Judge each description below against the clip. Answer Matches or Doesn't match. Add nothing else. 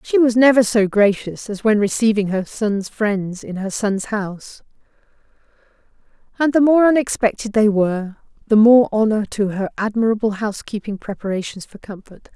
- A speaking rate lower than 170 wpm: Matches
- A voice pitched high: Matches